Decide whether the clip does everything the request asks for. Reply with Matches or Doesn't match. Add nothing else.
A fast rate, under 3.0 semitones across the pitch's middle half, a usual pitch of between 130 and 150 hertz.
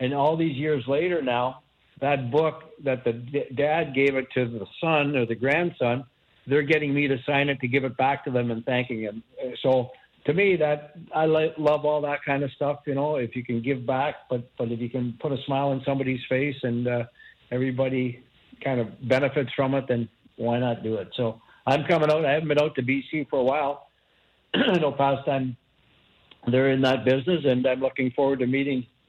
Matches